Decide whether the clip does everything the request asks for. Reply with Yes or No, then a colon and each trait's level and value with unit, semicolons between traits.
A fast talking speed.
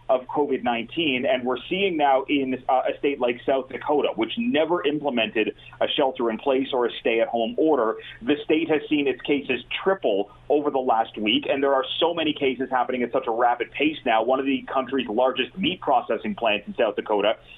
Yes: fast, 210 wpm